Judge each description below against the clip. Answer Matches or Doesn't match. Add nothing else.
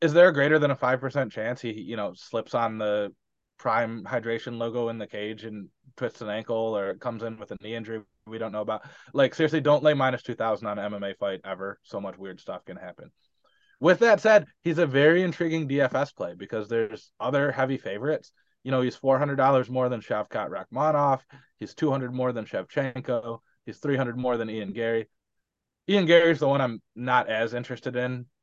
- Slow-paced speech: Doesn't match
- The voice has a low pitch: Matches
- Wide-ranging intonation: Doesn't match